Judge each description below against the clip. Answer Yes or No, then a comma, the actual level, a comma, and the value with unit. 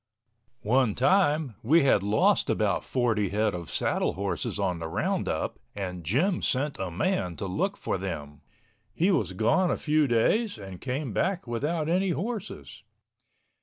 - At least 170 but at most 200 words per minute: No, average, 155 wpm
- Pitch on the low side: Yes, low, 125 Hz